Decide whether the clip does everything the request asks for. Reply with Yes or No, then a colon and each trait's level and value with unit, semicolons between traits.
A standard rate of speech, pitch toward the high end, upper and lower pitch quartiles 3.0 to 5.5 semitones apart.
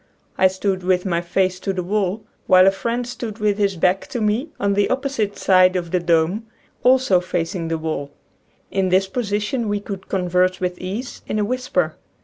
No: average, 190 wpm; high, 195 Hz; narrow, 2.6 semitones